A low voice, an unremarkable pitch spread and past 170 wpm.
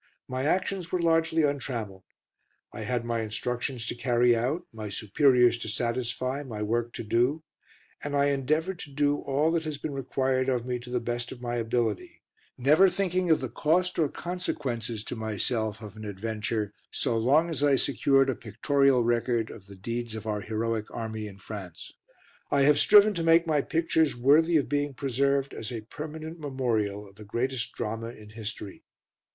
Yes: low, 125 Hz; average, 4.5 semitones; average, 180 wpm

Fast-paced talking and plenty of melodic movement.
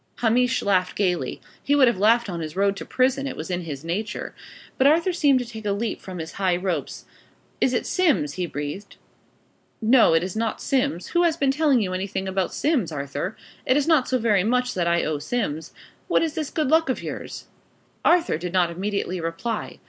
Yes: fast, 210 wpm; wide, 6.8 semitones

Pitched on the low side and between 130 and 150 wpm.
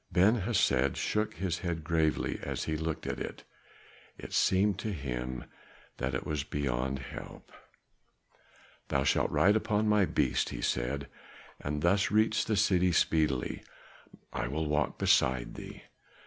Yes: very low, 80 Hz; average, 145 wpm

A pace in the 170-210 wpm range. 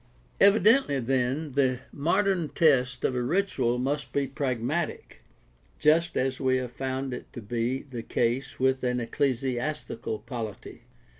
No: average, 145 wpm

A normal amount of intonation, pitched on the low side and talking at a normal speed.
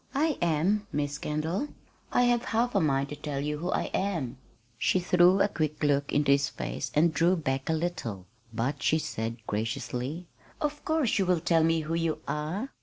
No: average, 4.6 semitones; medium, 160 Hz; average, 190 wpm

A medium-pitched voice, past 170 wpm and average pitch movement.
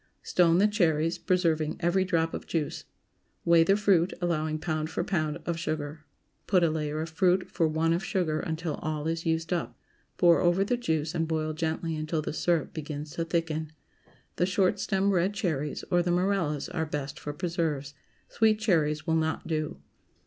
No: medium, 165 Hz; average, 185 wpm; narrow, 2.3 semitones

